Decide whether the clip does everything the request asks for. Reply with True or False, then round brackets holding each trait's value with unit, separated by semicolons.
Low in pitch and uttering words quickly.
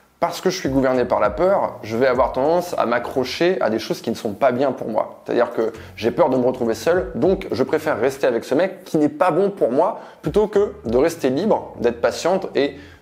False (170 Hz; 245 wpm)